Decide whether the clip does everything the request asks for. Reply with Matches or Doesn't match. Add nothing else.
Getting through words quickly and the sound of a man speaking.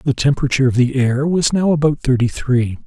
Matches